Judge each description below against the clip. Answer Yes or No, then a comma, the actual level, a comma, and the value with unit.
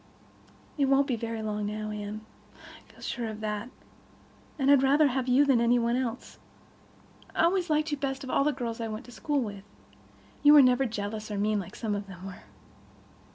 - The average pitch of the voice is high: Yes, high, 235 Hz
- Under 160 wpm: No, fast, 205 wpm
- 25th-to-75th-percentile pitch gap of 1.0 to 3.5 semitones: No, average, 4.3 semitones